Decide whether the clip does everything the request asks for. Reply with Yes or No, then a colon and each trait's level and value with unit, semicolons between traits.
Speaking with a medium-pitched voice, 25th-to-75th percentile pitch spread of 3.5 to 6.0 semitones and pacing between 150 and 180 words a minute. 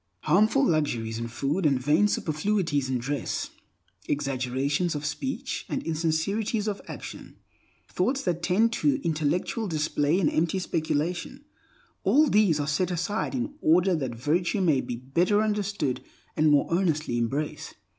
No: medium, 165 Hz; wide, 5.6 semitones; slow, 135 wpm